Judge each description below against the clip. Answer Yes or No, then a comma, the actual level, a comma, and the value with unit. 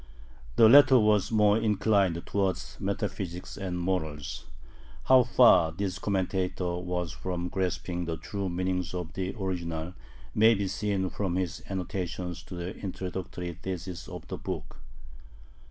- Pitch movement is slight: Yes, narrow, 2.2 semitones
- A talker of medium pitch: No, very low, 95 Hz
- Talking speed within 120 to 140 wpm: Yes, slow, 135 wpm